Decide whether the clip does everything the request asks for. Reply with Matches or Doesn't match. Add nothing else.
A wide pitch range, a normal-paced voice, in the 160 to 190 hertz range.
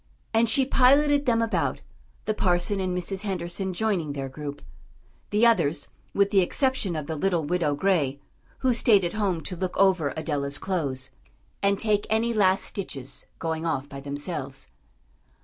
Matches